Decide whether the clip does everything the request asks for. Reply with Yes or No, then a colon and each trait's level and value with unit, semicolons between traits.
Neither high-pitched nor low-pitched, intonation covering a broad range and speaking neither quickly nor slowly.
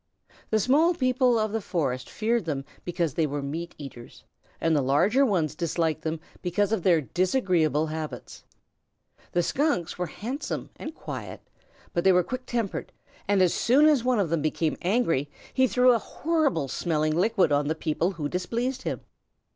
Yes: medium, 180 Hz; wide, 7.3 semitones; average, 170 wpm